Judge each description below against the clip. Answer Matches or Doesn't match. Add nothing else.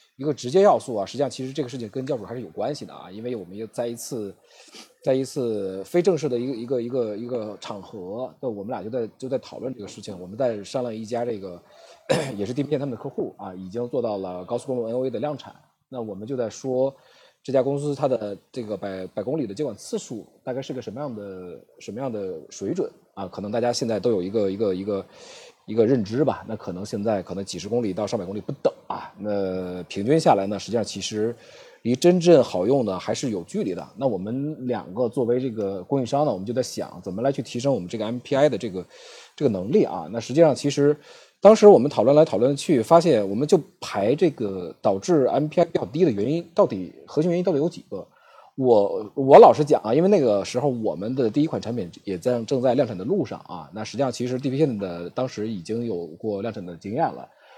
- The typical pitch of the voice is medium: Doesn't match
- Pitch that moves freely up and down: Matches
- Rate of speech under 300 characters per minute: Doesn't match